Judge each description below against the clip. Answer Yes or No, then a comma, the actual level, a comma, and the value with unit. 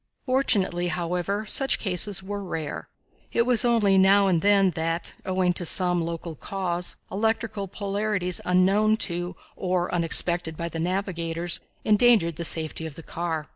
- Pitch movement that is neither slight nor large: Yes, average, 3.1 semitones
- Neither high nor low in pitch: Yes, medium, 180 Hz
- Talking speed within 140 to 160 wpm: Yes, average, 145 wpm